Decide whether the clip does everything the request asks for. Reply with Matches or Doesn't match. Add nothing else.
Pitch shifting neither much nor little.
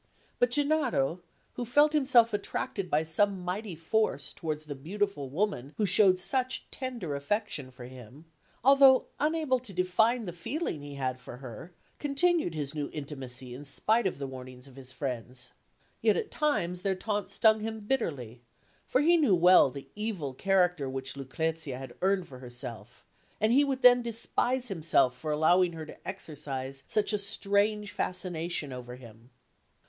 Doesn't match